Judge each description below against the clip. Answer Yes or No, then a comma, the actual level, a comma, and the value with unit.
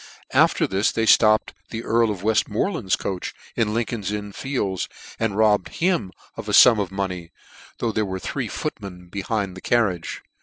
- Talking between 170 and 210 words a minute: Yes, average, 175 wpm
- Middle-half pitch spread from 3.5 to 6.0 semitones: No, average, 2.9 semitones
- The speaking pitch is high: No, low, 105 Hz